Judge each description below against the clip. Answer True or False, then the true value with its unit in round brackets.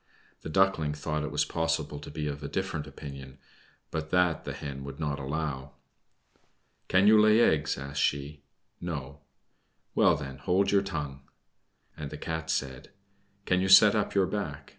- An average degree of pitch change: True (4.1 semitones)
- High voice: False (75 Hz)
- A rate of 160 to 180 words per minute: True (165 wpm)